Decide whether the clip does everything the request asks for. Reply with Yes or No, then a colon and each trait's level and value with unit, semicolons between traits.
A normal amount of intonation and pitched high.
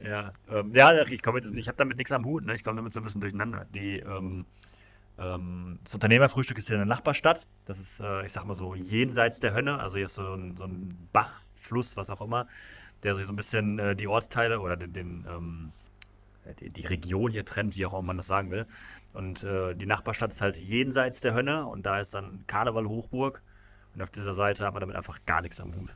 No: average, 3.3 semitones; low, 100 Hz